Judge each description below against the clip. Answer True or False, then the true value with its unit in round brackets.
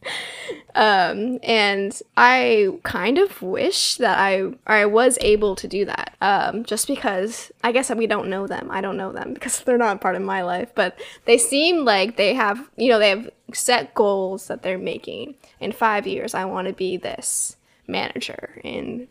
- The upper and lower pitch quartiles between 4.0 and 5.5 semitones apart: True (4.4 semitones)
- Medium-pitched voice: False (215 Hz)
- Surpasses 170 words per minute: True (185 wpm)